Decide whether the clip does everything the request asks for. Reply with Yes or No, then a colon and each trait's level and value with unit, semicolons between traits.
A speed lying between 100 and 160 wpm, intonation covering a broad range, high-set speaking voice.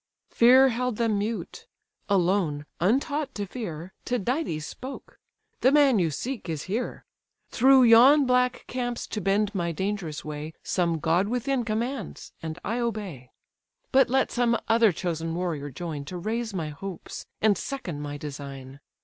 Yes: average, 145 wpm; wide, 7.0 semitones; high, 205 Hz